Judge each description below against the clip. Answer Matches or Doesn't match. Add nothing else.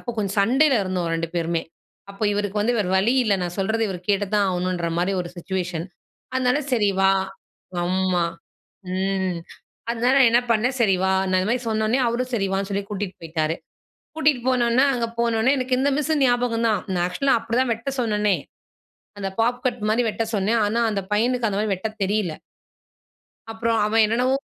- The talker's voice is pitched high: Matches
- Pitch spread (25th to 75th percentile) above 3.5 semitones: Matches